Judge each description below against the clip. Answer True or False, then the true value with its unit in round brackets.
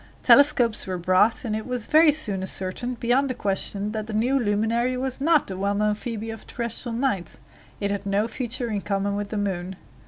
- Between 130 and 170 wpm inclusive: False (200 wpm)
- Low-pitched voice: False (220 Hz)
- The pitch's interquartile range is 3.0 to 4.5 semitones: True (3.7 semitones)